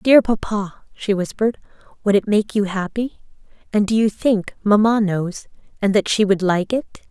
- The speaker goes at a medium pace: Yes, average, 175 wpm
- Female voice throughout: Yes, female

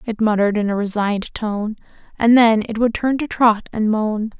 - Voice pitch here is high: Yes, high, 220 Hz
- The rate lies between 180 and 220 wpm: Yes, fast, 205 wpm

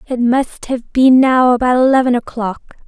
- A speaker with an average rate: Yes, average, 165 wpm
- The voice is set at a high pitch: Yes, very high, 250 Hz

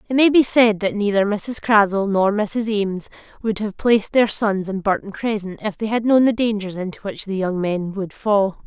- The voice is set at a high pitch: Yes, high, 205 Hz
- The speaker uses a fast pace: Yes, fast, 220 wpm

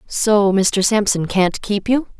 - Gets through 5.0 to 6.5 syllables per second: No, 3.5 syllables/s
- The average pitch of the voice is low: No, high, 205 Hz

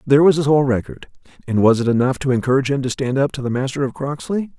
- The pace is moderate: No, fast, 260 wpm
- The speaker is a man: Yes, male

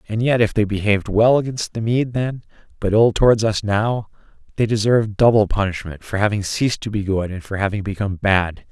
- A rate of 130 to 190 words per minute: No, fast, 205 wpm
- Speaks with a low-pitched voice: Yes, low, 105 Hz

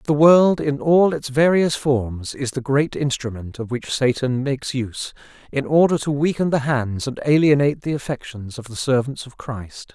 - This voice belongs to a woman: No, male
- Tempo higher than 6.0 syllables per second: No, 4.9 syllables/s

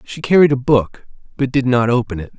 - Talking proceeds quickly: Yes, fast, 225 wpm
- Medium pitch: No, low, 125 Hz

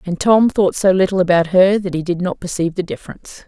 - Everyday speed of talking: No, fast, 240 wpm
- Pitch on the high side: No, medium, 180 Hz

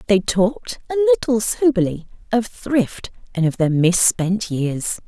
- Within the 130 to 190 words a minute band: Yes, average, 140 wpm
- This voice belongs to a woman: Yes, female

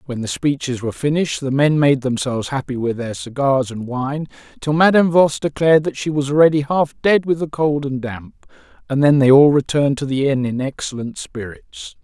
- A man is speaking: Yes, male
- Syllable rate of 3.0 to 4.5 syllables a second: No, 5.4 syllables/s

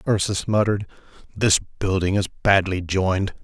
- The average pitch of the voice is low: Yes, very low, 95 Hz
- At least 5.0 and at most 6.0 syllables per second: Yes, 5.1 syllables/s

